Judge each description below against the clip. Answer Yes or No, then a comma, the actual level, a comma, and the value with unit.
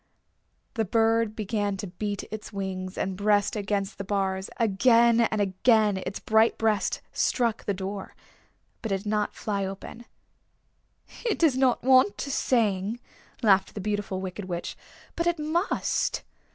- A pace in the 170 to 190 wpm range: No, average, 150 wpm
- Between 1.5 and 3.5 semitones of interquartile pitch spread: Yes, average, 2.9 semitones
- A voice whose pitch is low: No, high, 210 Hz